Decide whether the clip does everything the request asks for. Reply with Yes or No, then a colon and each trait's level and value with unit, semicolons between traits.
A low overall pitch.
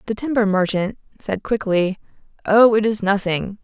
No: high, 205 Hz